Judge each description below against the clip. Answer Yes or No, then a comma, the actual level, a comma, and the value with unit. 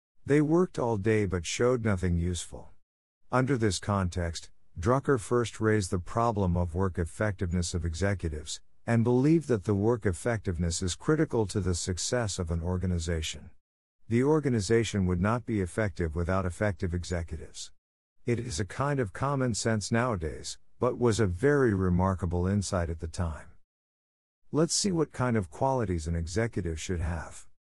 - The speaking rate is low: No, average, 155 wpm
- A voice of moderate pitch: No, very low, 95 Hz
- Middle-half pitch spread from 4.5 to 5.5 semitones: Yes, average, 5.2 semitones